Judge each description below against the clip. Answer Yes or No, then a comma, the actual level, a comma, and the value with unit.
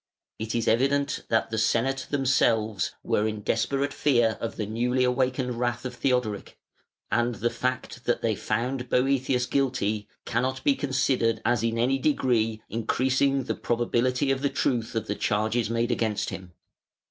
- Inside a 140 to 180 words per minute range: Yes, average, 160 wpm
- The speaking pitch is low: Yes, low, 120 Hz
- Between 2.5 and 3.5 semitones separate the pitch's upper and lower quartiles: Yes, average, 2.8 semitones